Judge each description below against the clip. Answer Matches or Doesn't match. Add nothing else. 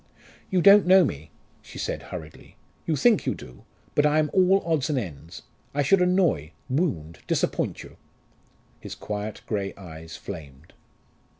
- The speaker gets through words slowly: Doesn't match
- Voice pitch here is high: Doesn't match